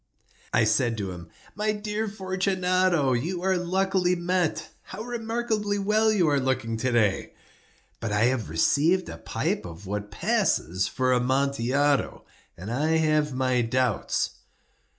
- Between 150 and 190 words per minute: No, average, 140 wpm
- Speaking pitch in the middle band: Yes, medium, 145 Hz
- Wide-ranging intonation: Yes, wide, 8.1 semitones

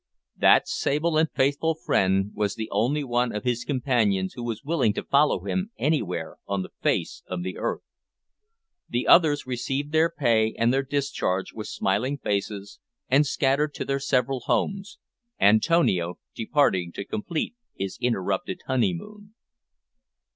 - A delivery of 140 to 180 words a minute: Yes, average, 145 wpm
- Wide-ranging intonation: Yes, wide, 6.2 semitones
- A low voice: Yes, low, 125 Hz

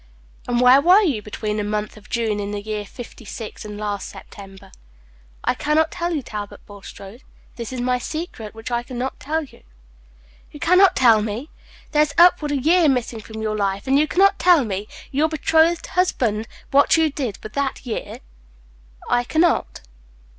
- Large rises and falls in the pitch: Yes, wide, 6.4 semitones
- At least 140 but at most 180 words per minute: No, average, 195 wpm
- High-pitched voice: Yes, high, 245 Hz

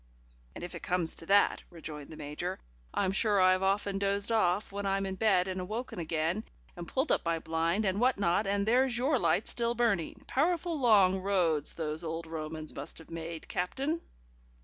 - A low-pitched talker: No, high, 190 Hz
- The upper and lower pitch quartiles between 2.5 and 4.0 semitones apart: No, average, 4.5 semitones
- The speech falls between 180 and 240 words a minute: Yes, average, 190 wpm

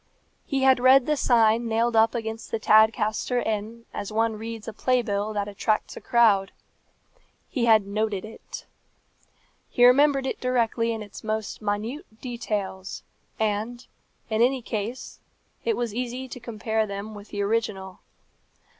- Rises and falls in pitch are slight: Yes, narrow, 2.2 semitones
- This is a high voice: Yes, high, 225 Hz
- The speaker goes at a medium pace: Yes, average, 150 wpm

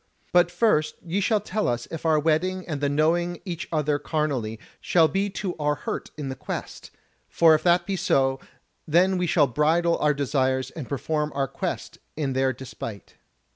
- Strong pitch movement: No, average, 3.8 semitones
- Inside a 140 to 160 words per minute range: No, average, 180 wpm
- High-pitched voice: No, medium, 155 Hz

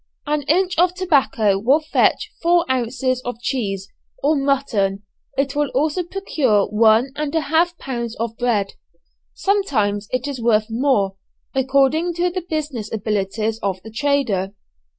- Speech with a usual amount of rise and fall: No, wide, 5.9 semitones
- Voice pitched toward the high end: Yes, very high, 260 Hz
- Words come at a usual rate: Yes, average, 145 wpm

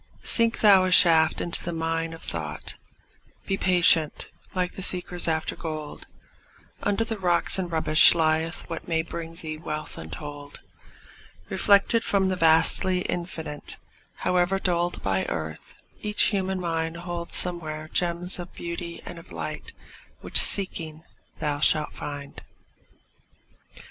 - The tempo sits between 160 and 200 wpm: No, slow, 135 wpm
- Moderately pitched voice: Yes, medium, 170 Hz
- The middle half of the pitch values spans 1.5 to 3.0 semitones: Yes, narrow, 2.5 semitones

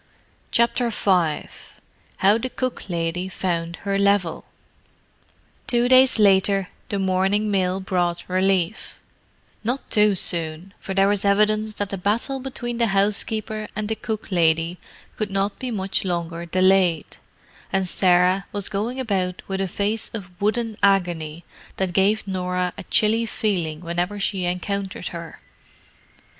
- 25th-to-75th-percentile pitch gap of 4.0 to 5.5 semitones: No, average, 2.9 semitones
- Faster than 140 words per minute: No, slow, 135 wpm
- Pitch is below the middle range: No, high, 195 Hz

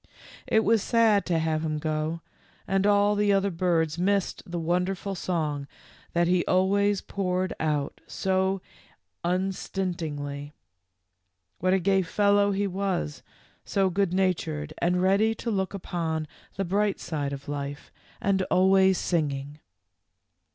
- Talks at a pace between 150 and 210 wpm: No, slow, 135 wpm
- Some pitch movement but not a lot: Yes, average, 3.6 semitones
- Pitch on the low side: No, medium, 185 Hz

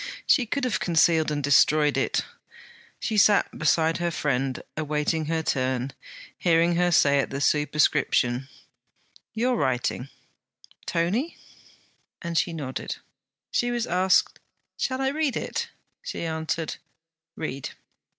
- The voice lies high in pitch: No, medium, 160 Hz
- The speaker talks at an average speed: No, slow, 120 wpm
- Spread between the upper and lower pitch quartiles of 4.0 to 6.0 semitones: Yes, average, 4.8 semitones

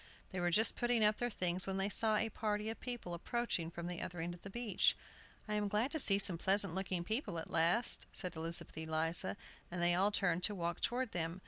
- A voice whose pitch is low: No, high, 190 Hz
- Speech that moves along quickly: Yes, fast, 230 wpm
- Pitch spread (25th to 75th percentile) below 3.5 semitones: No, average, 3.9 semitones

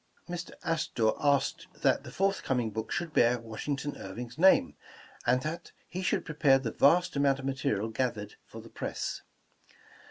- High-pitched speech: No, low, 135 Hz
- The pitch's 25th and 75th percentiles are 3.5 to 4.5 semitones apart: No, average, 5.3 semitones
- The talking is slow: No, average, 165 wpm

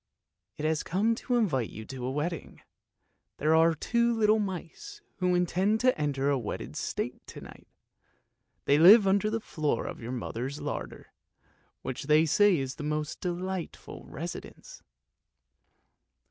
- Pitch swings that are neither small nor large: No, wide, 6.3 semitones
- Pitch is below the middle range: No, medium, 165 Hz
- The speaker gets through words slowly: No, average, 145 wpm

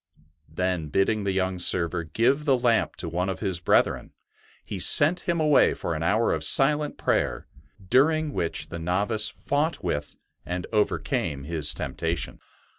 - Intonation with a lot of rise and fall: Yes, wide, 8.1 semitones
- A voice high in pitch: No, very low, 95 Hz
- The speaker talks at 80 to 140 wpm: No, average, 155 wpm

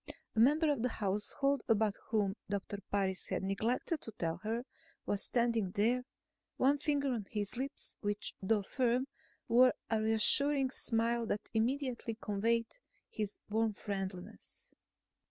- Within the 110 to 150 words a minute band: Yes, slow, 135 wpm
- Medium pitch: No, high, 225 Hz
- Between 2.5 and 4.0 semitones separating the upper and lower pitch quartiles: Yes, average, 3.6 semitones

